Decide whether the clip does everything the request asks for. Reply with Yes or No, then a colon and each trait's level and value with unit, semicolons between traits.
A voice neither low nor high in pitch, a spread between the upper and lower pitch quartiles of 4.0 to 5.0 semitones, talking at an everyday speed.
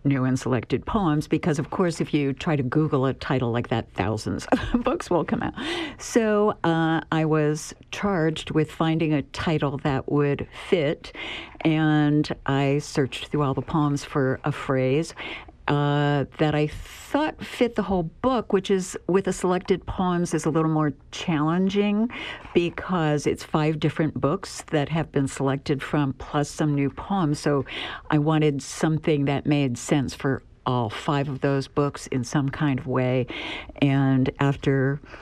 No: medium, 150 Hz; average, 2.9 semitones; average, 165 wpm